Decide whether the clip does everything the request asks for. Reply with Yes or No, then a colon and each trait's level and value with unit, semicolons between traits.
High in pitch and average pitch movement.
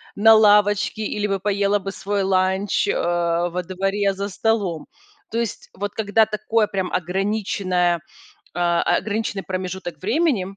No: high, 200 Hz; narrow, 2.2 semitones